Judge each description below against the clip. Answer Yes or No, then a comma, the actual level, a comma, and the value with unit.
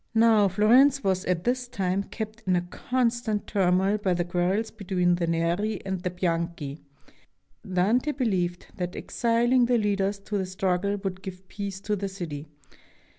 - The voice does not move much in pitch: No, average, 3.5 semitones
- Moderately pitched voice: No, high, 195 Hz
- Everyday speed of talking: Yes, average, 160 wpm